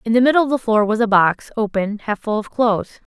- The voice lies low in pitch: No, high, 220 Hz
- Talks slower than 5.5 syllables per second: No, 5.9 syllables/s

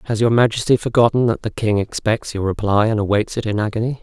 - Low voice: Yes, low, 110 Hz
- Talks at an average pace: No, fast, 225 wpm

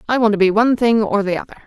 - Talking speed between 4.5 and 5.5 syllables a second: No, 7.9 syllables/s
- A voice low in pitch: No, high, 215 Hz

